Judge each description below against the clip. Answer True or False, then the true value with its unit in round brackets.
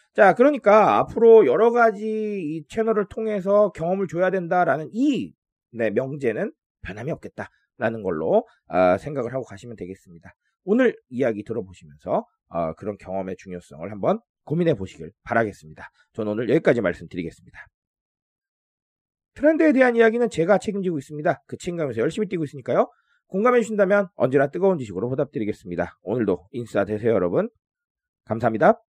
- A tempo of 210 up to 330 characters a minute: False (385 characters per minute)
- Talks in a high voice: False (180 Hz)